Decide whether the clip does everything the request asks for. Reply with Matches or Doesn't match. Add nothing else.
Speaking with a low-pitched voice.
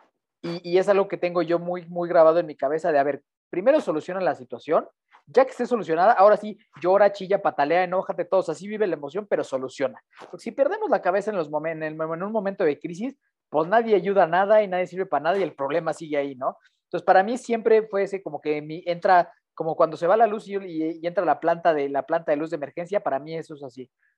Doesn't match